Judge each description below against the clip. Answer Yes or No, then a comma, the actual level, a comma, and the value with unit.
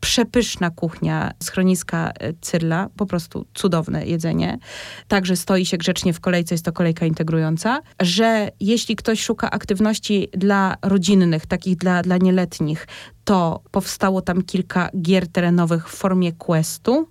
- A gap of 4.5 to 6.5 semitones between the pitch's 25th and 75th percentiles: No, average, 2.7 semitones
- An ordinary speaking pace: Yes, average, 135 wpm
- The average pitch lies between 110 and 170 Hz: No, medium, 185 Hz